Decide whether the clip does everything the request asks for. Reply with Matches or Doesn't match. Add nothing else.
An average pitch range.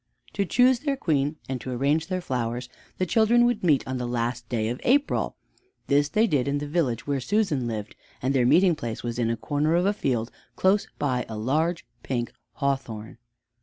Doesn't match